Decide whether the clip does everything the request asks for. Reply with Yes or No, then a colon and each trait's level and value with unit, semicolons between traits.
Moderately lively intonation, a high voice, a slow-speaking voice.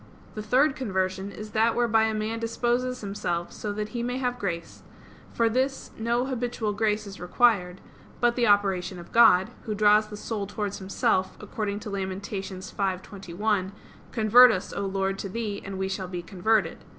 No: average, 3.1 semitones; high, 210 Hz; average, 175 wpm